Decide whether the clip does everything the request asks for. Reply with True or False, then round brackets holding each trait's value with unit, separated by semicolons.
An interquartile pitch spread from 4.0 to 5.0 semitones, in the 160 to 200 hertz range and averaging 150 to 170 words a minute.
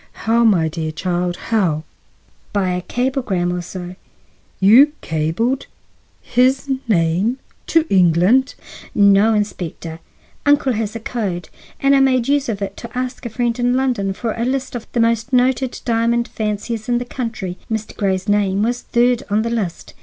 False (4.6 semitones; 225 Hz; 155 wpm)